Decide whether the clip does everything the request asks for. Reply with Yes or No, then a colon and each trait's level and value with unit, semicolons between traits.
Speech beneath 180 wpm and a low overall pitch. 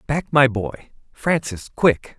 Yes: slow, 135 wpm; low, 130 Hz